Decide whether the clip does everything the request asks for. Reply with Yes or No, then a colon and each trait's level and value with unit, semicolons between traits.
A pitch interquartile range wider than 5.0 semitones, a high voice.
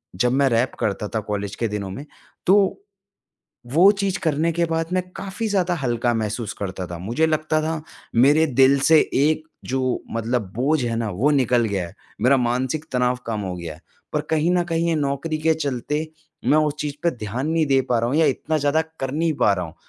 No: wide, 5.5 semitones; low, 135 Hz